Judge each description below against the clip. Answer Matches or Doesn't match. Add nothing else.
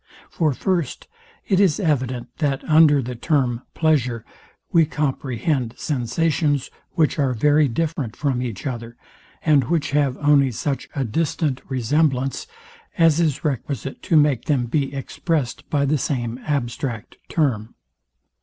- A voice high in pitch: Doesn't match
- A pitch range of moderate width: Matches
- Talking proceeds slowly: Matches